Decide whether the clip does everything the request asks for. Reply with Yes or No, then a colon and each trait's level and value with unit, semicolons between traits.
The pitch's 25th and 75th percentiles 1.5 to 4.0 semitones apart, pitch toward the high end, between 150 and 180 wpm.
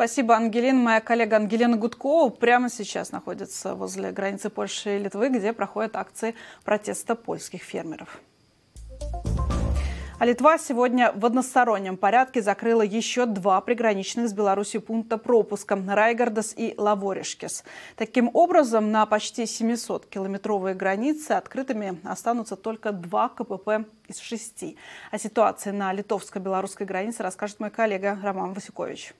No: average, 2.8 semitones; high, 220 Hz; average, 125 wpm